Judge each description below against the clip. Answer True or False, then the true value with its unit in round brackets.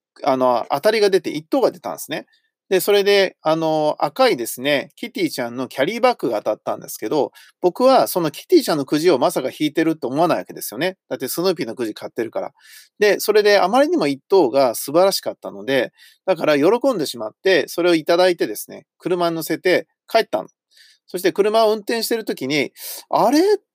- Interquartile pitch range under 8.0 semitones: False (8.4 semitones)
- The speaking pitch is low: False (195 Hz)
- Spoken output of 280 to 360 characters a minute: False (415 characters per minute)